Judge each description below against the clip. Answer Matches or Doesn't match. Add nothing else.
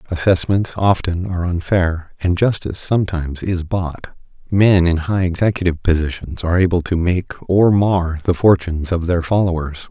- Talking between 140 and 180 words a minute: Matches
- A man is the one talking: Matches